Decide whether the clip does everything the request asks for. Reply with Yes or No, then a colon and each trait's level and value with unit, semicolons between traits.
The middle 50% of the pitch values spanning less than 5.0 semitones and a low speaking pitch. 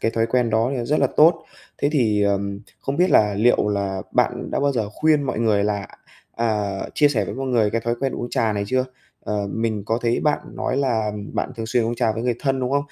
Yes: average, 3.8 semitones; low, 115 Hz